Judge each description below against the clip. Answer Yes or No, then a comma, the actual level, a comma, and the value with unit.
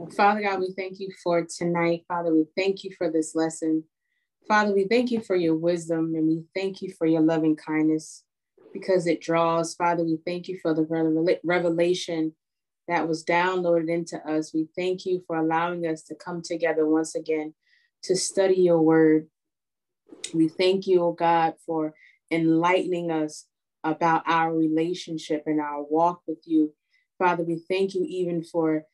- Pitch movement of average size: No, narrow, 2.2 semitones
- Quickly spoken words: No, average, 170 wpm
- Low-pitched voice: No, medium, 170 Hz